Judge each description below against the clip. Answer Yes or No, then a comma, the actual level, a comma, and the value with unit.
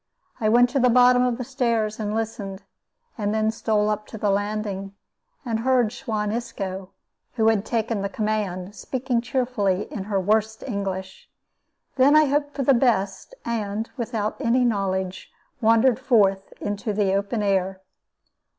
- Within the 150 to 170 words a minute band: Yes, average, 155 wpm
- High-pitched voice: Yes, high, 215 Hz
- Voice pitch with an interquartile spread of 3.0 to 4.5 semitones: Yes, average, 3.3 semitones